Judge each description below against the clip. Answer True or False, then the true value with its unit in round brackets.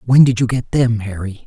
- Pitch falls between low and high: False (115 Hz)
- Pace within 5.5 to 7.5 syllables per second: False (4.9 syllables/s)